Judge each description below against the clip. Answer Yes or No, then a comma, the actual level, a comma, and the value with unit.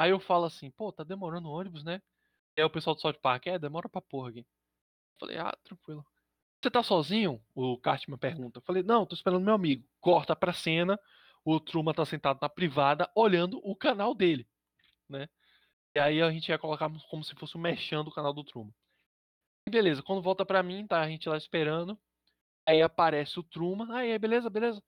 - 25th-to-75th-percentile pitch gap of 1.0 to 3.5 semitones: No, average, 4.2 semitones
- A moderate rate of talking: No, fast, 200 wpm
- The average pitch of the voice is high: No, medium, 160 Hz